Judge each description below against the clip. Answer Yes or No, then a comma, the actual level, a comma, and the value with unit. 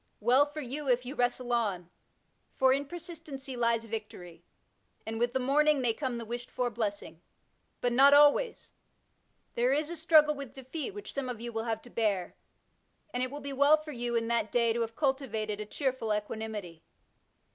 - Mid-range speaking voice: No, high, 245 Hz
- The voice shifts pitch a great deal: No, average, 3.9 semitones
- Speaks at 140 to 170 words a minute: No, average, 190 wpm